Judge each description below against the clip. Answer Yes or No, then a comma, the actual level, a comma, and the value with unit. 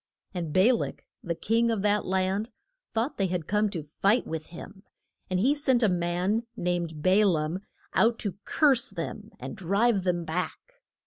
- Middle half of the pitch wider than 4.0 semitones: Yes, average, 4.4 semitones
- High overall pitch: Yes, high, 195 Hz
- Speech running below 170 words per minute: No, average, 175 wpm